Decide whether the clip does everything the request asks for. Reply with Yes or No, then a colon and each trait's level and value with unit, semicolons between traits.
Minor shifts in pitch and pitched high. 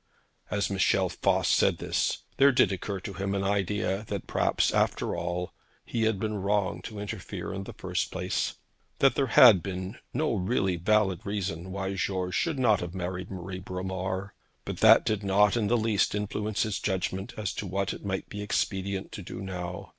No: narrow, 1.9 semitones; low, 100 Hz